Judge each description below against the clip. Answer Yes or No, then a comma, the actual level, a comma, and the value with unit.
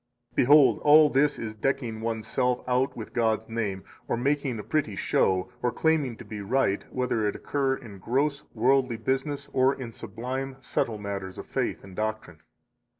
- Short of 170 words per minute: No, average, 175 wpm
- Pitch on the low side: Yes, low, 120 Hz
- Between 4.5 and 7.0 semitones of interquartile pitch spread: No, average, 3.7 semitones